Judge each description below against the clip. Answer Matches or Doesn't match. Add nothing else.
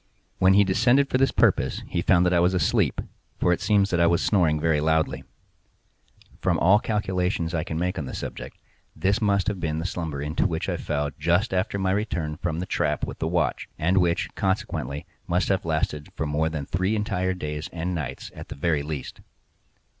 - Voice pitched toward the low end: Matches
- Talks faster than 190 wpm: Matches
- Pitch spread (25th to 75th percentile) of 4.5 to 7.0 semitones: Doesn't match